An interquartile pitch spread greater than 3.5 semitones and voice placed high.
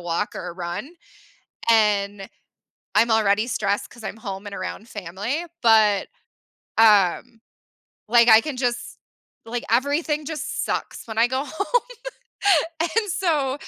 Yes: average, 4.6 semitones; high, 225 Hz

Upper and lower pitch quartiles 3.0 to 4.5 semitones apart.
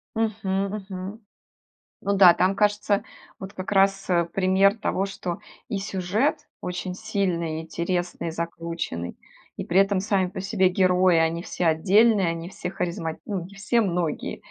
No: narrow, 2.5 semitones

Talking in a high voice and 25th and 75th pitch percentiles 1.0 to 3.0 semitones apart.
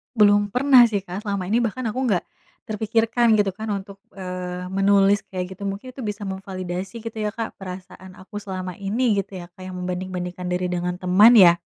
Yes: high, 195 Hz; average, 2.7 semitones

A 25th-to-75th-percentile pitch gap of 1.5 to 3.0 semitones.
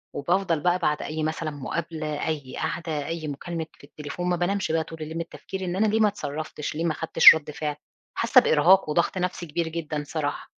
Yes: narrow, 2.5 semitones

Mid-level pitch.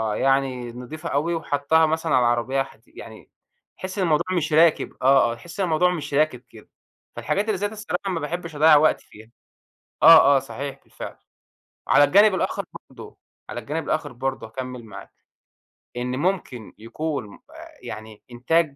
Yes: medium, 145 Hz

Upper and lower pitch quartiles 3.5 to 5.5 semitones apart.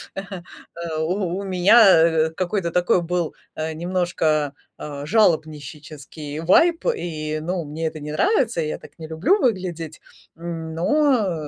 No: average, 3.1 semitones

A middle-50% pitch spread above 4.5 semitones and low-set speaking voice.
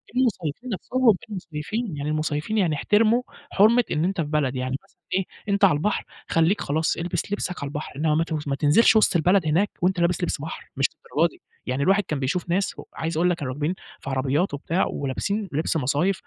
No: average, 5.0 semitones; medium, 165 Hz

